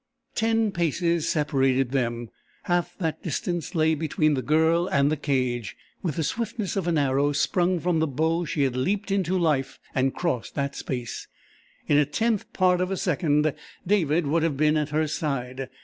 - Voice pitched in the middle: Yes, medium, 155 Hz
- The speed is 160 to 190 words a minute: Yes, average, 180 wpm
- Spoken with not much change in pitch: No, average, 4.1 semitones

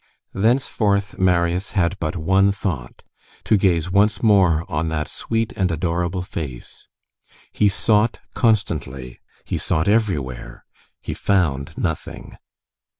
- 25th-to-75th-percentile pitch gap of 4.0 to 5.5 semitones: Yes, average, 4.3 semitones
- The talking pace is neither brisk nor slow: No, slow, 110 wpm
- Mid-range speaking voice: No, very low, 90 Hz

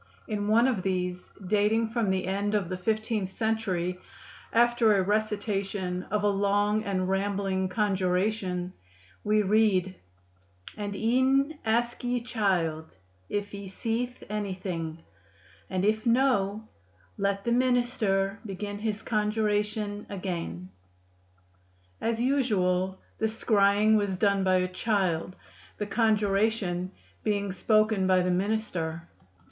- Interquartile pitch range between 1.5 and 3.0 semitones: Yes, average, 2.7 semitones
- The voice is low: No, high, 205 Hz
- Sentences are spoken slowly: Yes, slow, 120 wpm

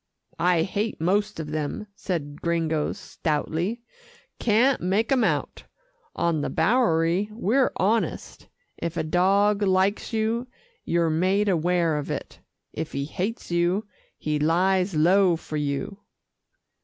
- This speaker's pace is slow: Yes, slow, 130 wpm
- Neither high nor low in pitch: Yes, medium, 180 Hz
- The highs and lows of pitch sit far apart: No, average, 4.3 semitones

